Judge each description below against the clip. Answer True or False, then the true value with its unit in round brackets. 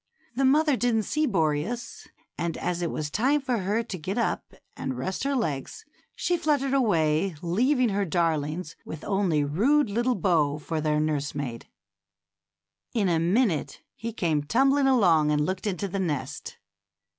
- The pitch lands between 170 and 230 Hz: True (190 Hz)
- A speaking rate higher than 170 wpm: False (155 wpm)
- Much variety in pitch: True (7.9 semitones)